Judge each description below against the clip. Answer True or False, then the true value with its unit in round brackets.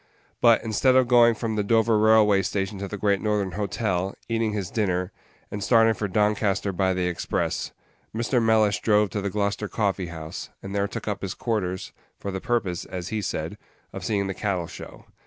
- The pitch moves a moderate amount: False (2.3 semitones)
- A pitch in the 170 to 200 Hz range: False (105 Hz)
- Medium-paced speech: True (195 wpm)